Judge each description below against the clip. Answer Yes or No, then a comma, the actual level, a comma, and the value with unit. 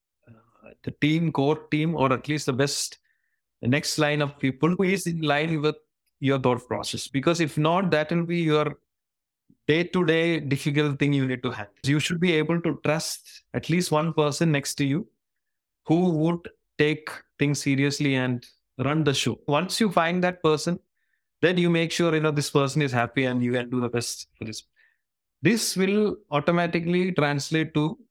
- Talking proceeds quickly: No, average, 185 wpm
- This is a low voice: No, medium, 150 Hz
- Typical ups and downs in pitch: Yes, average, 3.2 semitones